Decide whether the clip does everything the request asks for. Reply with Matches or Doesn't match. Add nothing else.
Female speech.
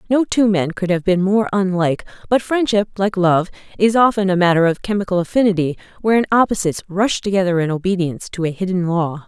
Matches